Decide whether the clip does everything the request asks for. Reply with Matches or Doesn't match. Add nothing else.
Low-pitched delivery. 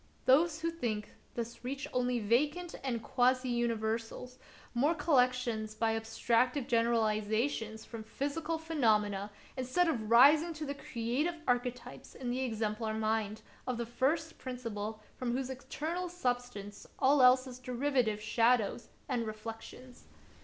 Doesn't match